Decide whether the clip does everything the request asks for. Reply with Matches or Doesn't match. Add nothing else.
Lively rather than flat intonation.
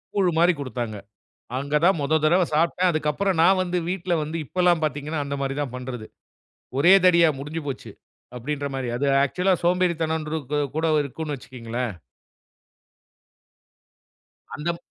Doesn't match